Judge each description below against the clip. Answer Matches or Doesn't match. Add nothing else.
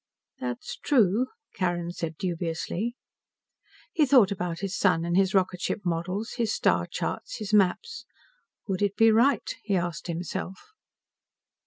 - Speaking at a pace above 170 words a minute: Doesn't match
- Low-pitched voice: Doesn't match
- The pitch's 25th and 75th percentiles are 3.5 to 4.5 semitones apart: Matches